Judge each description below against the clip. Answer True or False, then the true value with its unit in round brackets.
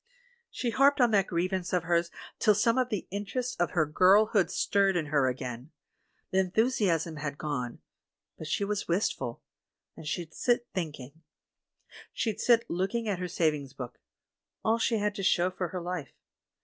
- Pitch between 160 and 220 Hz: True (185 Hz)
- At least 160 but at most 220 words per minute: True (175 wpm)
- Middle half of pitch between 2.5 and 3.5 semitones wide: False (5.0 semitones)